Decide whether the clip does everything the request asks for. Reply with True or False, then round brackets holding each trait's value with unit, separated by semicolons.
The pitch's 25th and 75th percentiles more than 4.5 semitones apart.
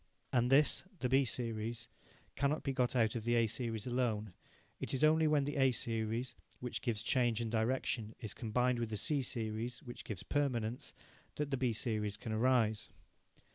False (2.8 semitones)